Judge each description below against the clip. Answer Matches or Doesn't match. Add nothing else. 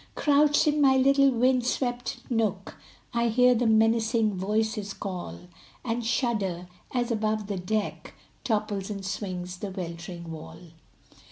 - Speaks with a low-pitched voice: Doesn't match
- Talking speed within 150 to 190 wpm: Doesn't match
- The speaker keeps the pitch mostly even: Doesn't match